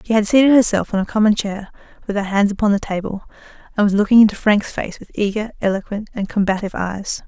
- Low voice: No, high, 205 Hz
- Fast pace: Yes, fast, 215 wpm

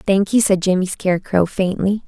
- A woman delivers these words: Yes, female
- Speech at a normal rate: Yes, average, 175 wpm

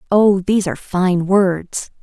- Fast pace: No, average, 150 wpm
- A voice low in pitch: No, high, 190 Hz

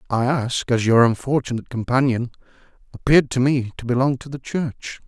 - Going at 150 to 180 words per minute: Yes, average, 165 wpm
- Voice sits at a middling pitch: No, low, 125 Hz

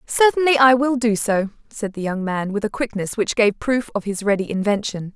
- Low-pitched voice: No, high, 220 Hz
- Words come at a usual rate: No, fast, 220 wpm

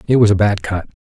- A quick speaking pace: Yes, fast, 290 wpm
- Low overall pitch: Yes, low, 105 Hz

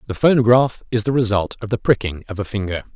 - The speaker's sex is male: Yes, male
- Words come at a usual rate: No, fast, 225 wpm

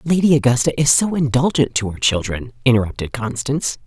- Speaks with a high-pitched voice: No, low, 130 Hz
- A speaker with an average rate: Yes, average, 170 wpm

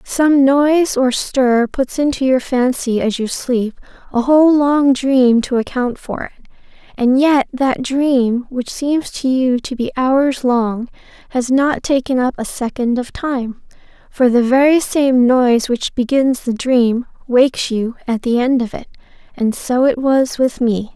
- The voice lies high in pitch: Yes, very high, 255 Hz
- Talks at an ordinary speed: Yes, average, 175 wpm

